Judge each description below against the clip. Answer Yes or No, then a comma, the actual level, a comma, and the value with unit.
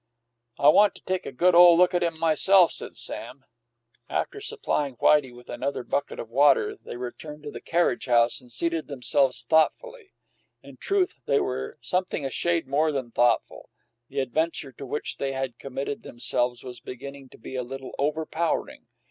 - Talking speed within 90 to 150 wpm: No, average, 175 wpm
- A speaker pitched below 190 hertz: Yes, medium, 140 Hz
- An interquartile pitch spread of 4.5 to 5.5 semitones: Yes, average, 4.8 semitones